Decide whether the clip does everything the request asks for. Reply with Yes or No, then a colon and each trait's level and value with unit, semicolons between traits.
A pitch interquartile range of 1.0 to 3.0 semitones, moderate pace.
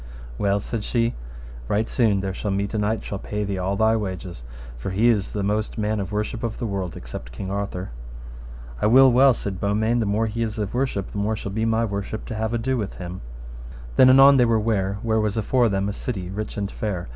No: narrow, 2.4 semitones; fast, 230 wpm